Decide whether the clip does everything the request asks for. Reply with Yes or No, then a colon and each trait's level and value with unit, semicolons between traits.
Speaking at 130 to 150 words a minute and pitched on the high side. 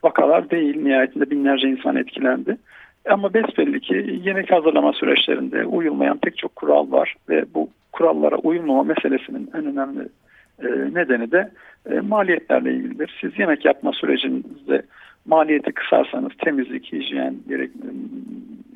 No: average, 115 wpm; high, 195 Hz